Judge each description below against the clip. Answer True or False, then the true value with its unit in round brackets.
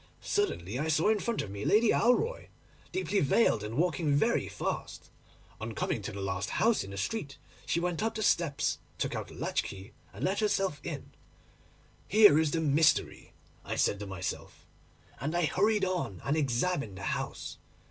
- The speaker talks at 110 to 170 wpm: False (180 wpm)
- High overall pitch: False (160 Hz)